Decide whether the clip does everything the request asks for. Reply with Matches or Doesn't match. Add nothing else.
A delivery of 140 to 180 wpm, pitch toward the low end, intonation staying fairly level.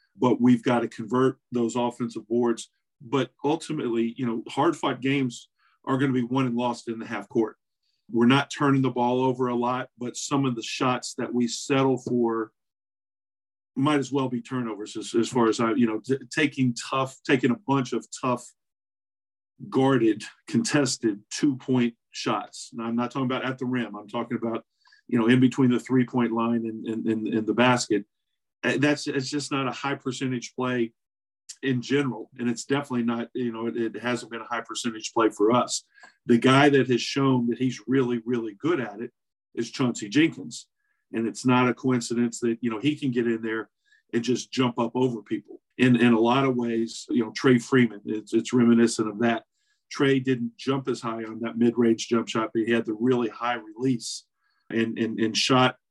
Doesn't match